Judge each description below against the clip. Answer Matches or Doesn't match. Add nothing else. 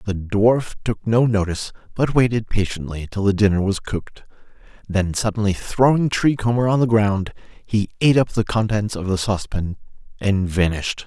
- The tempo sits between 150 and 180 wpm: Matches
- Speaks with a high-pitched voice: Doesn't match